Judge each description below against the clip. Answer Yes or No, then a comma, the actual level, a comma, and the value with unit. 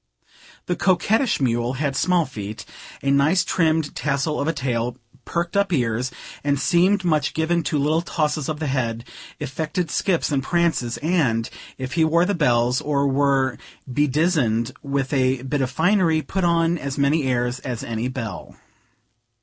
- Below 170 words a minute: Yes, average, 160 wpm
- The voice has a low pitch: No, medium, 145 Hz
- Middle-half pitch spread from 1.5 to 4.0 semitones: No, average, 4.4 semitones